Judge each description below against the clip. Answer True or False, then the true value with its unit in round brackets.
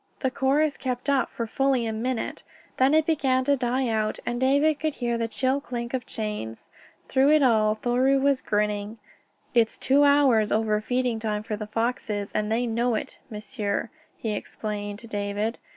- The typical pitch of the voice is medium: False (235 Hz)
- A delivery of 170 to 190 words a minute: True (180 wpm)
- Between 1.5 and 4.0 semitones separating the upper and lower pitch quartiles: True (3.7 semitones)